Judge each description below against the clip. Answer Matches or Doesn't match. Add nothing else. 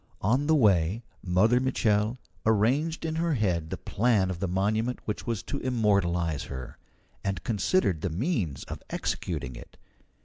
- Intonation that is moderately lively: Doesn't match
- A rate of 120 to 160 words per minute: Matches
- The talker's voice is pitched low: Matches